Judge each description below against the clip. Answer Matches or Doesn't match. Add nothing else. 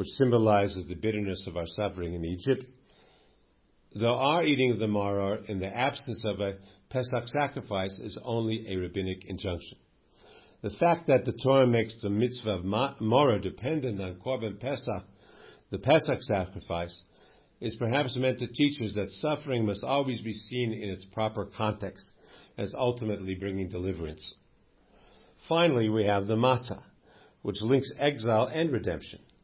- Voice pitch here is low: Matches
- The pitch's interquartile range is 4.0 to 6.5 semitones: Matches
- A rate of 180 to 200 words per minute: Doesn't match